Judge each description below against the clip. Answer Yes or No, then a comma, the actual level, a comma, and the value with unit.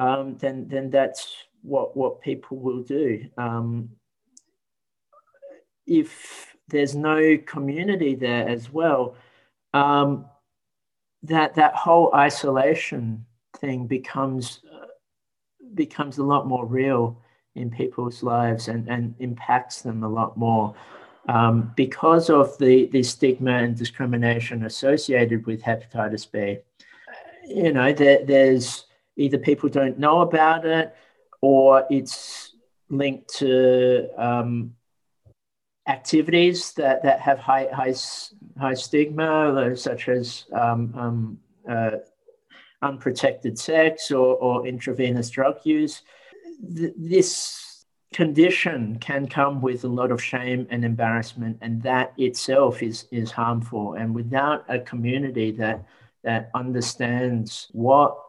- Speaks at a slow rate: Yes, slow, 115 wpm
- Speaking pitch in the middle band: No, low, 130 Hz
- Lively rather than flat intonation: No, average, 3.2 semitones